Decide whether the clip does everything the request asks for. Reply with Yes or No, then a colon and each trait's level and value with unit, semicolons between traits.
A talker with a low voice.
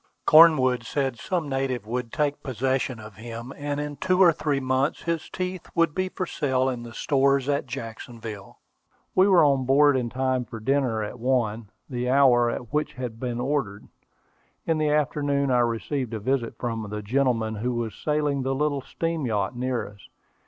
Yes: low, 130 Hz